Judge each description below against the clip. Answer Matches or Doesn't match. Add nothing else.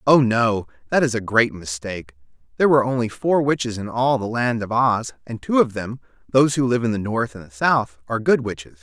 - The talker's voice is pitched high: Doesn't match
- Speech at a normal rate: Doesn't match